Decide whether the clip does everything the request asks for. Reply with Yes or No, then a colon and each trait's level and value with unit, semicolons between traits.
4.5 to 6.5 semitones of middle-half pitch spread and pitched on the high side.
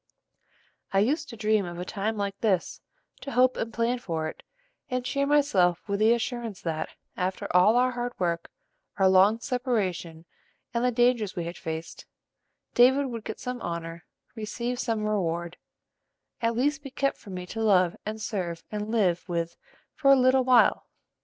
Yes: wide, 5.5 semitones; high, 215 Hz